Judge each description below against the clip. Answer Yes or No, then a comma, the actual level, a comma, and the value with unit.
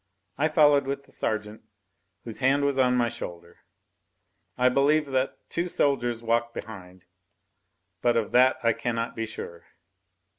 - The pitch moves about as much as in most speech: Yes, average, 3.5 semitones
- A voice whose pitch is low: Yes, low, 120 Hz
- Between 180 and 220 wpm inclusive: No, average, 145 wpm